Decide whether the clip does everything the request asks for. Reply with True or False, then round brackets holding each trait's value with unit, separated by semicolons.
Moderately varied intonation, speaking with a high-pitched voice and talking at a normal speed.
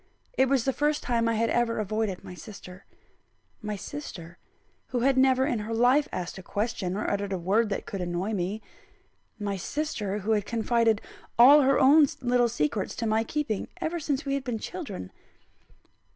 True (4.6 semitones; 225 Hz; 180 wpm)